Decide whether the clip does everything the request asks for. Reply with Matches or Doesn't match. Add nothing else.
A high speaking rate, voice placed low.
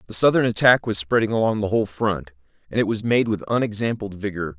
Matches